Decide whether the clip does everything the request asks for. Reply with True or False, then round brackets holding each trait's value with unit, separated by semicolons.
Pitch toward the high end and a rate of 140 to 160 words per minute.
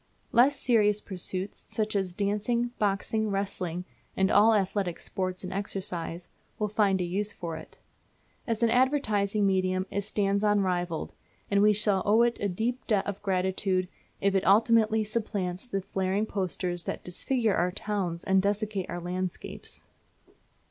True (200 Hz; 150 wpm)